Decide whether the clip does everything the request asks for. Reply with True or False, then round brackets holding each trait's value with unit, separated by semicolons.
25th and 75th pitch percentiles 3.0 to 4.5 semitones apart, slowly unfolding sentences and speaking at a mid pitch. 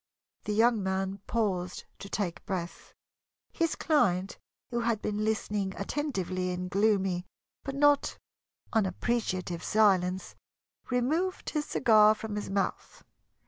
False (4.0 semitones; 115 wpm; 205 Hz)